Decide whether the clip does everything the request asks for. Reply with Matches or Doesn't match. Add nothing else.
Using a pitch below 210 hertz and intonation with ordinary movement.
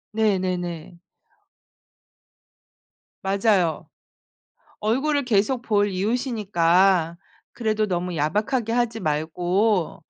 Matches